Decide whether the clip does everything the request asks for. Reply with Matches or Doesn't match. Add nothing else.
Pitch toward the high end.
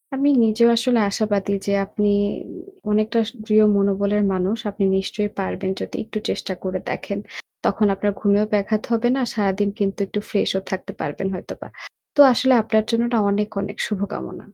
Matches